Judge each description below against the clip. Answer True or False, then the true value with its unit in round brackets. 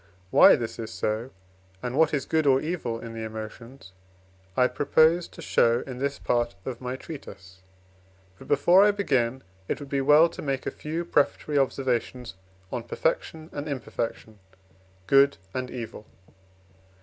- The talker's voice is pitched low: True (130 Hz)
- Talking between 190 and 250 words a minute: False (155 wpm)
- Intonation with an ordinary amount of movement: True (4.0 semitones)